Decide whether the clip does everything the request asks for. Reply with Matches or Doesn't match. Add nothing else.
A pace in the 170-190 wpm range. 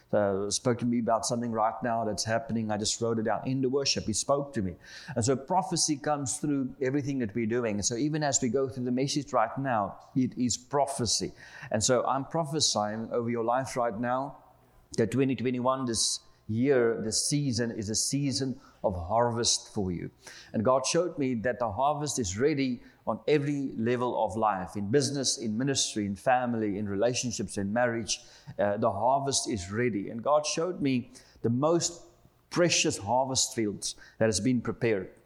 Matches